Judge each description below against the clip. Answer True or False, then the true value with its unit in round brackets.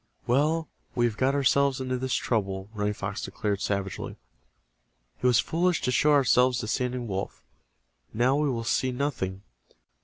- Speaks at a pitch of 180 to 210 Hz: False (125 Hz)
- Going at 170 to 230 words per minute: False (155 wpm)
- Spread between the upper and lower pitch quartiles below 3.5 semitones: False (4.7 semitones)